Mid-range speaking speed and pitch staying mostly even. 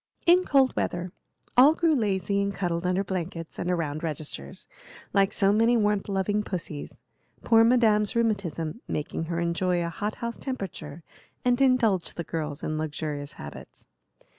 No: average, 150 wpm; average, 5.3 semitones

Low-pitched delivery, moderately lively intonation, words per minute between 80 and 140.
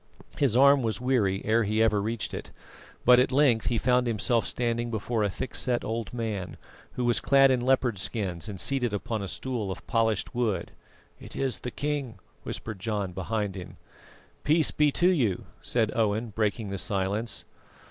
No: low, 115 Hz; average, 3.3 semitones; average, 175 wpm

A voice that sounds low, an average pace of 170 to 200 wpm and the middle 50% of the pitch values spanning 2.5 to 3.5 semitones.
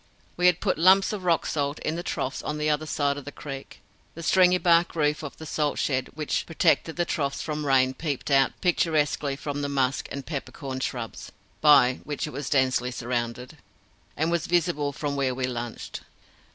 No: medium, 145 Hz; average, 190 wpm; average, 3.1 semitones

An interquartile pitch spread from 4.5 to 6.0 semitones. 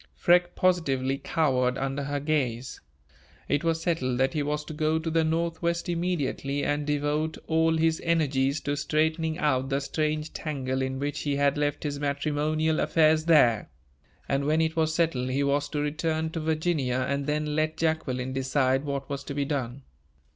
No: narrow, 2.5 semitones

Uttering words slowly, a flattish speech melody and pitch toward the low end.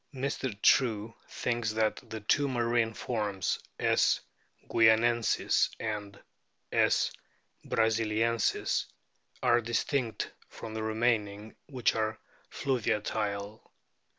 Yes: slow, 90 wpm; narrow, 1.7 semitones; low, 110 Hz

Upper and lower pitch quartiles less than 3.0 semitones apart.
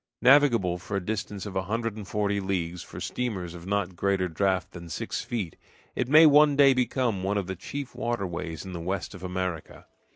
No: average, 4.4 semitones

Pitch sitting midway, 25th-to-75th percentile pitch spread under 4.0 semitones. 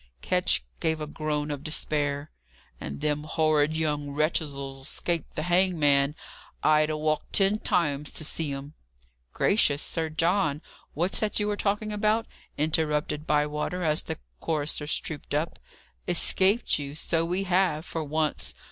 Yes: medium, 155 Hz; narrow, 2.6 semitones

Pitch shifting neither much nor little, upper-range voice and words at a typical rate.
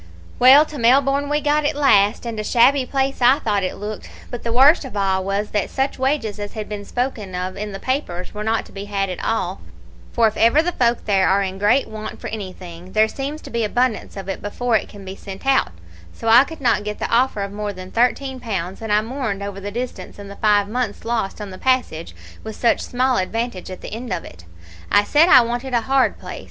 No: average, 4.3 semitones; high, 220 Hz; fast, 240 wpm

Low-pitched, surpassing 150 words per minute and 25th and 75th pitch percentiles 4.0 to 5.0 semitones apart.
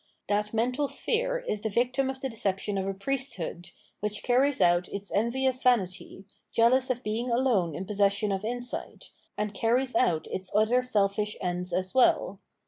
No: high, 215 Hz; average, 165 wpm; average, 4.4 semitones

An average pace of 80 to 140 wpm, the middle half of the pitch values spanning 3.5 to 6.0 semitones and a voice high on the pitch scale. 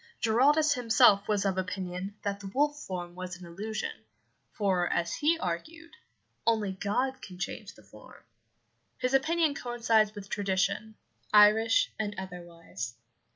Yes: slow, 135 wpm; average, 4.6 semitones; high, 205 Hz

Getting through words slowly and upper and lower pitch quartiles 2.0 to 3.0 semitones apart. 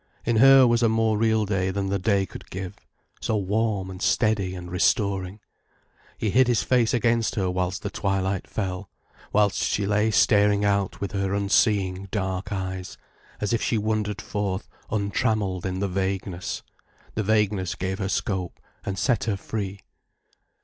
No: average, 165 wpm; narrow, 2.4 semitones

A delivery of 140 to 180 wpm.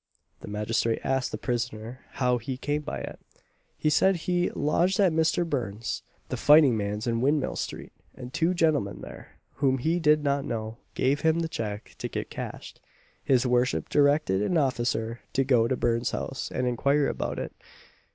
Yes: average, 175 wpm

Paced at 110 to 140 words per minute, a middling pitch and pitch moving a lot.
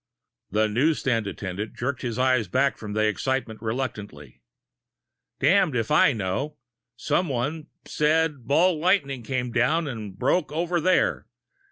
No: slow, 135 wpm; low, 130 Hz; wide, 5.7 semitones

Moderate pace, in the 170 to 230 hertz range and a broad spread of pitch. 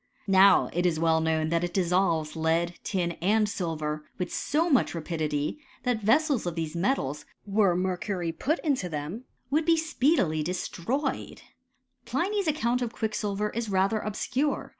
Yes: average, 160 wpm; high, 190 Hz; wide, 6.4 semitones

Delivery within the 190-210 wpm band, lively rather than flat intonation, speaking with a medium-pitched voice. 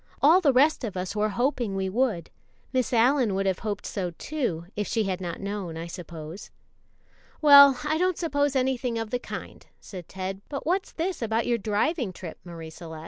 No: average, 195 wpm; wide, 6.7 semitones; high, 220 Hz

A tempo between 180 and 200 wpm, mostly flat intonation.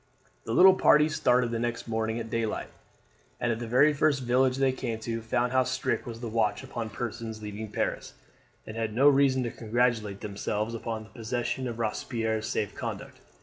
Yes: average, 190 wpm; narrow, 2.3 semitones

